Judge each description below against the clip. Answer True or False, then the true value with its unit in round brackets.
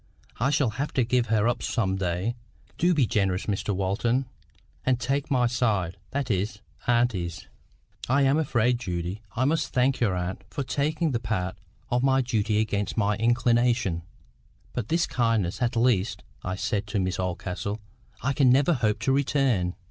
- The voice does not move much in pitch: False (4.7 semitones)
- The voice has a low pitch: True (115 Hz)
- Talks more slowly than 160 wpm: False (165 wpm)